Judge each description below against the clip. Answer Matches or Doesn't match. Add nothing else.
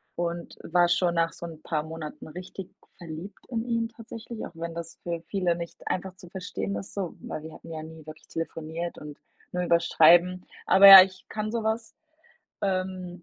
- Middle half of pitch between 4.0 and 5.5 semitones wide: Doesn't match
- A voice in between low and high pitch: Matches